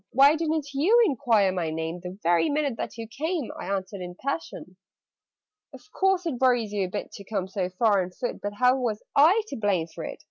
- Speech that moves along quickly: Yes, fast, 220 wpm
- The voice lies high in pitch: Yes, high, 220 Hz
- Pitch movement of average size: No, wide, 7.3 semitones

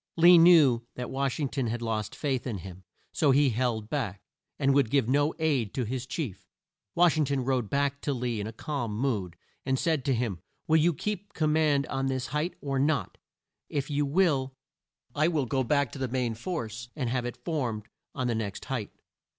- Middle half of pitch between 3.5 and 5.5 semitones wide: Yes, average, 3.8 semitones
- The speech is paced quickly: Yes, fast, 210 wpm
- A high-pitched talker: No, low, 135 Hz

